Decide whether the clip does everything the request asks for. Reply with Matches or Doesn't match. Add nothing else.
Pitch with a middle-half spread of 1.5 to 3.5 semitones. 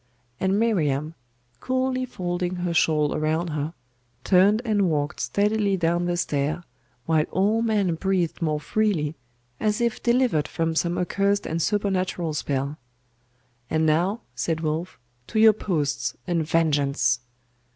Doesn't match